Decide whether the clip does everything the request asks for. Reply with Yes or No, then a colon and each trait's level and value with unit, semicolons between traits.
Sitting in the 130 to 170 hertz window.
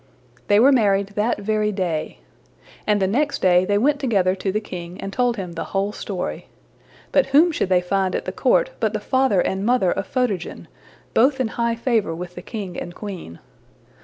No: high, 205 Hz